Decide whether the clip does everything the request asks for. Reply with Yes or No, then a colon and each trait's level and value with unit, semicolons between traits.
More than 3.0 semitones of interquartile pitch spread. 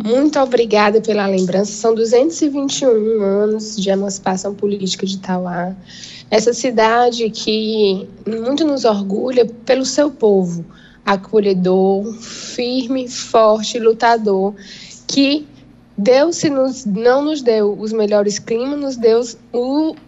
Yes: average, 3.8 semitones